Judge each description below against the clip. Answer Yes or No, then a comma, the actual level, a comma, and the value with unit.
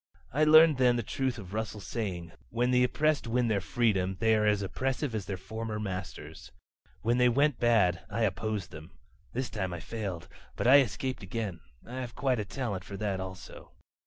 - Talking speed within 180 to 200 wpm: Yes, average, 190 wpm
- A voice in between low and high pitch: No, low, 110 Hz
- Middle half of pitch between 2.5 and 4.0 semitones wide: No, average, 4.4 semitones